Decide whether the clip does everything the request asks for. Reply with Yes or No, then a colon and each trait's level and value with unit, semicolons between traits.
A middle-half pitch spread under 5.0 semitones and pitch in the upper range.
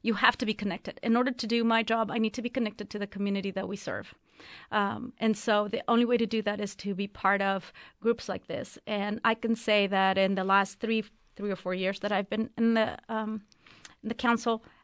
Yes: narrow, 2.4 semitones; high, 215 Hz